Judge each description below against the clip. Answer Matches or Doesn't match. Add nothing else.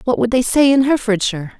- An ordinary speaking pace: Doesn't match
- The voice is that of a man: Doesn't match